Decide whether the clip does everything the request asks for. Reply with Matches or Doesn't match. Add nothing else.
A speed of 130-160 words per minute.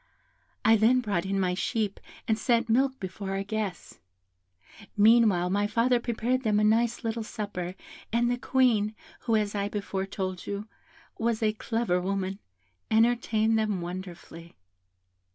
Matches